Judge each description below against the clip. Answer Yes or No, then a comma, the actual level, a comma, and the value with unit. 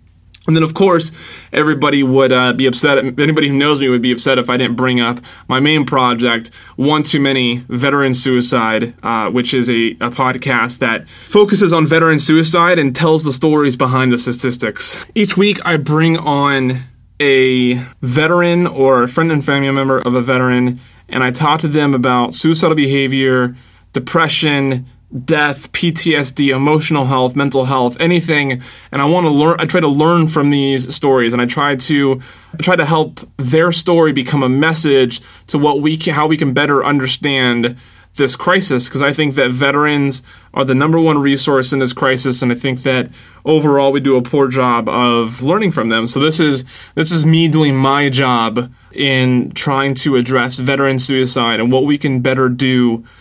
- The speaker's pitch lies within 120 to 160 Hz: Yes, low, 135 Hz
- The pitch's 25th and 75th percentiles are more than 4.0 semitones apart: No, average, 3.3 semitones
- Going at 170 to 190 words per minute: Yes, average, 180 wpm